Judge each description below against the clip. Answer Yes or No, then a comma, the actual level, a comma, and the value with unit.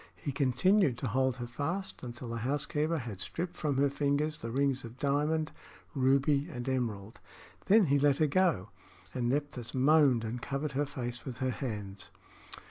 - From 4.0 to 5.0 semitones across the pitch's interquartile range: No, average, 3.4 semitones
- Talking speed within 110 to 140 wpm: No, average, 170 wpm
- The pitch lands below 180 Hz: Yes, low, 135 Hz